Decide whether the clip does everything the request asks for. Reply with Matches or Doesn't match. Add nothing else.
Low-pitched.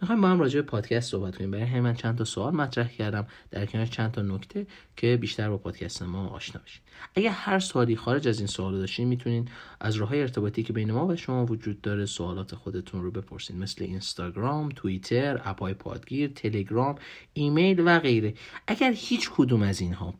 Matches